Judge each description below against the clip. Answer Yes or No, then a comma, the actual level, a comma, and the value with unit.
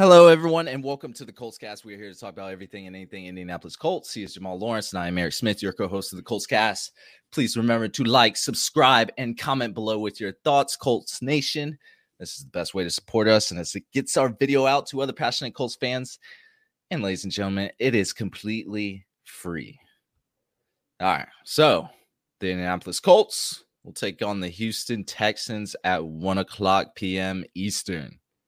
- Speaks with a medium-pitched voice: No, low, 105 Hz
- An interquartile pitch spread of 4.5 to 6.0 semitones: Yes, average, 5.1 semitones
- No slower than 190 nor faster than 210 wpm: Yes, average, 195 wpm